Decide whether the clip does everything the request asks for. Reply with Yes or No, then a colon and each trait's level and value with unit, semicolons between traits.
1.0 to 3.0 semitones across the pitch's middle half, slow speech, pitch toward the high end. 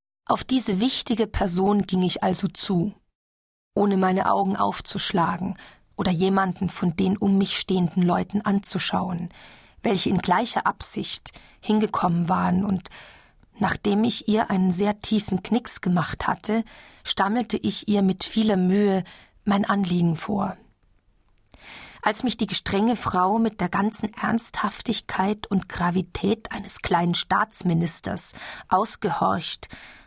Yes: narrow, 2.5 semitones; slow, 120 wpm; high, 195 Hz